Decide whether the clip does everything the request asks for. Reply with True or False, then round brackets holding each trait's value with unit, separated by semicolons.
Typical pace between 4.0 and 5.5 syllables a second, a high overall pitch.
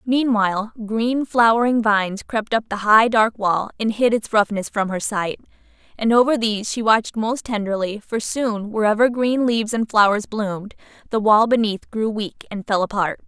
True (4.9 syllables/s; 220 Hz)